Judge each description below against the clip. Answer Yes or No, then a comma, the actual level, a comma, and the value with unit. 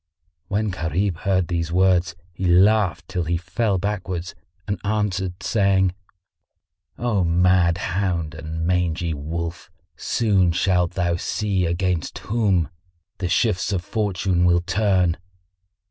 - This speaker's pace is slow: Yes, slow, 120 wpm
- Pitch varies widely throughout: No, narrow, 2.4 semitones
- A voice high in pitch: No, very low, 90 Hz